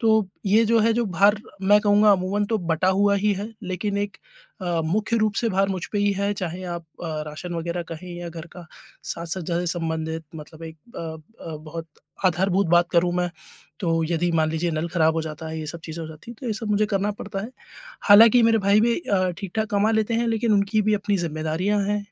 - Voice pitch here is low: No, high, 190 Hz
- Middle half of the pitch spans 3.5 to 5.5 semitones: Yes, average, 3.9 semitones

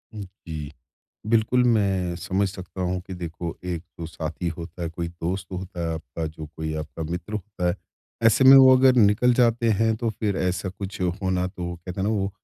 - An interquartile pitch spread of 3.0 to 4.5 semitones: Yes, average, 3.7 semitones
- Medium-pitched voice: No, very low, 90 Hz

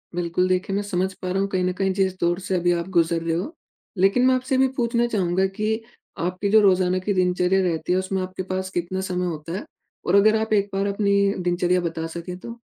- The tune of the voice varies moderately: No, narrow, 2.1 semitones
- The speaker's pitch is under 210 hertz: Yes, medium, 185 Hz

